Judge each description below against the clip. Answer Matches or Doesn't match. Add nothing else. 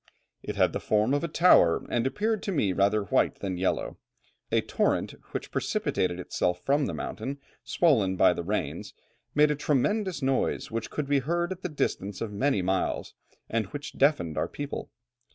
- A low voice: Matches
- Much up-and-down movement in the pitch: Matches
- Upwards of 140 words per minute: Matches